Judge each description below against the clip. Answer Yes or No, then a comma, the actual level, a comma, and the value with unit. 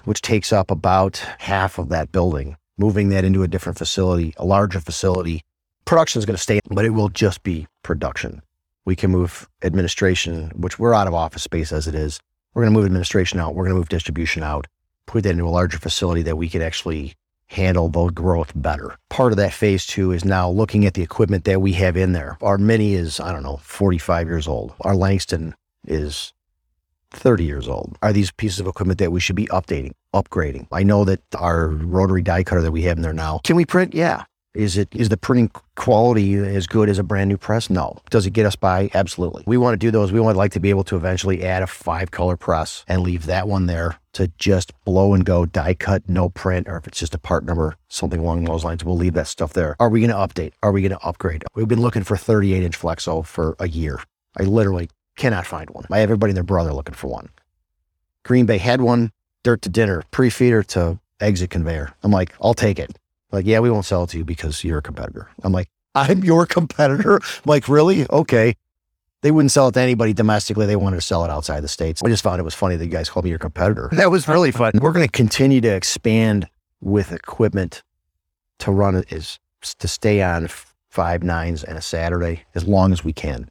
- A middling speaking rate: No, fast, 230 wpm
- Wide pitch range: No, average, 3.9 semitones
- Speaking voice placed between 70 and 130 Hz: Yes, very low, 95 Hz